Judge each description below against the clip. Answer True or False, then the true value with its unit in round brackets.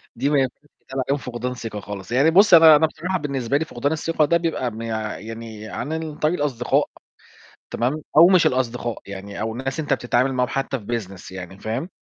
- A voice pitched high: False (130 Hz)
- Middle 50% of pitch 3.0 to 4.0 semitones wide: False (5.1 semitones)